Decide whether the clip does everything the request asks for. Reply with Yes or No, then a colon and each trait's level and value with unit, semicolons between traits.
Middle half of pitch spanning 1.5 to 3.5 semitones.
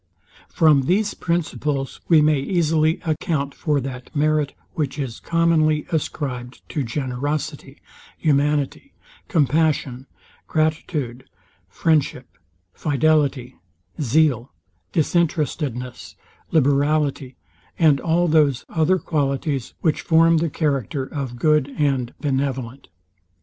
Yes: average, 2.8 semitones